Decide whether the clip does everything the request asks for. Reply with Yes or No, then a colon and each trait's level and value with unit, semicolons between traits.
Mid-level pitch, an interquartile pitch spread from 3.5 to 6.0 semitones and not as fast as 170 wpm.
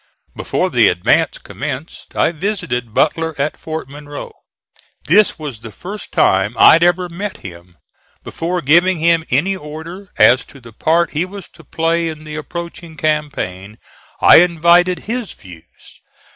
Yes: medium, 160 Hz; average, 3.8 semitones; average, 150 wpm